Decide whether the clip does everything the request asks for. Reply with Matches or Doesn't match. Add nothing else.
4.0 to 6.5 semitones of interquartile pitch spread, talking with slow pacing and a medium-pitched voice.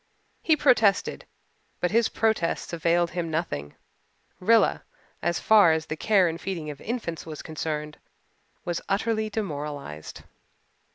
Matches